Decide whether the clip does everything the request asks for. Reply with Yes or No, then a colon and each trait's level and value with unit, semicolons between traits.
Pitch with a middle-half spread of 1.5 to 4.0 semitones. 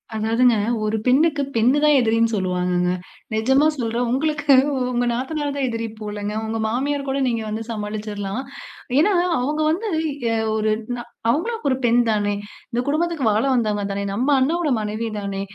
No: average, 4.9 semitones